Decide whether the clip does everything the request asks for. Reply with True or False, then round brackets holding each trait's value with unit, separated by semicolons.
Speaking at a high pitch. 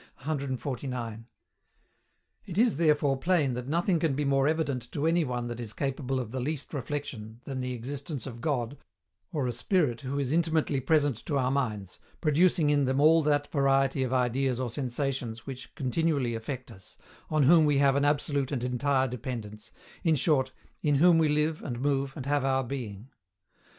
False (135 Hz)